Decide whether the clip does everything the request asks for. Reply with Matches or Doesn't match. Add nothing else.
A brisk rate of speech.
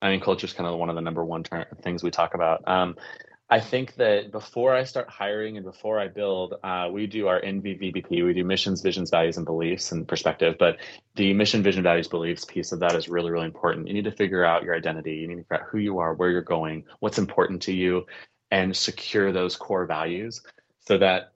Matches